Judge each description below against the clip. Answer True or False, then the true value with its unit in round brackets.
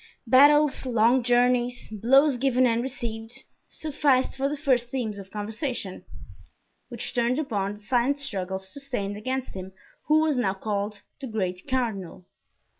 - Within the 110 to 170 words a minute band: True (140 wpm)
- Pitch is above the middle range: True (240 Hz)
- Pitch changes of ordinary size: True (4.4 semitones)